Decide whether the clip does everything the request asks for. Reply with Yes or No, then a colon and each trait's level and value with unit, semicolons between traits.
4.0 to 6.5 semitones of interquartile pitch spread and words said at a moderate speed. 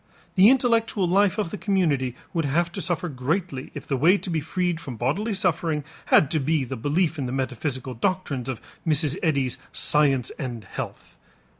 Yes: wide, 5.6 semitones; average, 180 wpm